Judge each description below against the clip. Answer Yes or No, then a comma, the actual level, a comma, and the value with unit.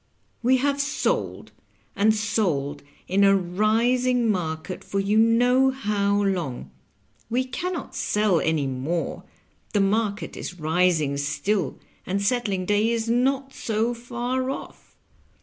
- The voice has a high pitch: Yes, high, 210 Hz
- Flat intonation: No, average, 5.0 semitones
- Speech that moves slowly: Yes, slow, 130 wpm